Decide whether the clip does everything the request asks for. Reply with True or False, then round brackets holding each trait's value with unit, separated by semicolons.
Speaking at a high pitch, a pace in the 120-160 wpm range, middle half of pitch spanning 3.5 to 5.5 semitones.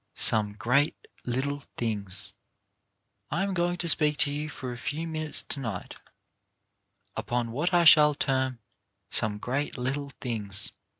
False (135 Hz; 145 wpm; 4.6 semitones)